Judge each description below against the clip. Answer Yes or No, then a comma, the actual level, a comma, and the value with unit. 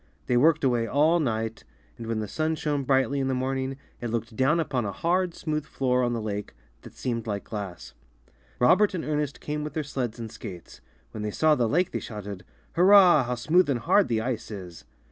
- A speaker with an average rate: No, fast, 210 wpm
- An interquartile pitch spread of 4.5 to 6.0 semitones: Yes, average, 5.2 semitones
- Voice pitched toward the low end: Yes, low, 130 Hz